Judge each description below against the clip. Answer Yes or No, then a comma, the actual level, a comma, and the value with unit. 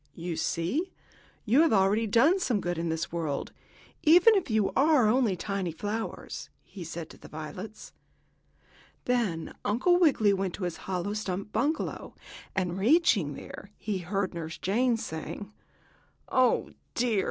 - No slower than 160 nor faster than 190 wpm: No, average, 150 wpm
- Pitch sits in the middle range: No, high, 205 Hz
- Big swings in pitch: Yes, wide, 5.9 semitones